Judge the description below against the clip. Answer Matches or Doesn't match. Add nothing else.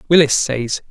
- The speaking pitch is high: Doesn't match